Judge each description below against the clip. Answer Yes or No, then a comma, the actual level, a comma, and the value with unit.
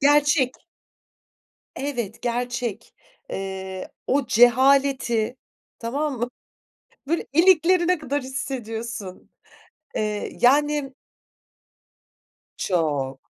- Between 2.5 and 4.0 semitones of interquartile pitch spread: No, average, 4.7 semitones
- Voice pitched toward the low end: No, very high, 250 Hz